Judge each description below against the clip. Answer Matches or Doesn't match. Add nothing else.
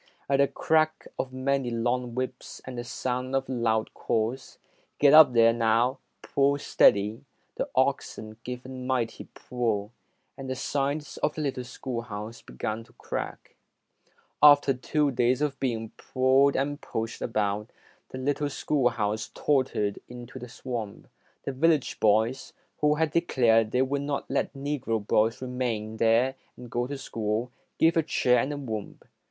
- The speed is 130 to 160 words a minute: Matches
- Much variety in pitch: Doesn't match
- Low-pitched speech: Matches